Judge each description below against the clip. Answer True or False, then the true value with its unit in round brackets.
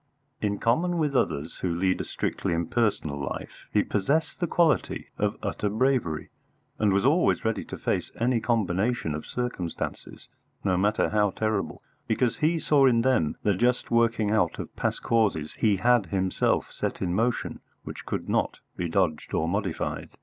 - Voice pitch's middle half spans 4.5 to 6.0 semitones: True (5.1 semitones)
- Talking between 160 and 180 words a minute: True (165 wpm)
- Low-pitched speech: True (105 Hz)